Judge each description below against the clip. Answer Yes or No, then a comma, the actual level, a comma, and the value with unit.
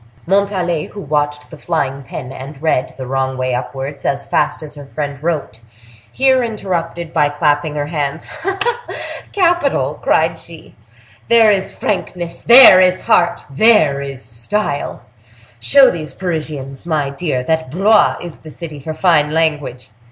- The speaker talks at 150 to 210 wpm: No, average, 140 wpm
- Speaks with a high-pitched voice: No, medium, 155 Hz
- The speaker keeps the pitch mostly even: No, average, 4.3 semitones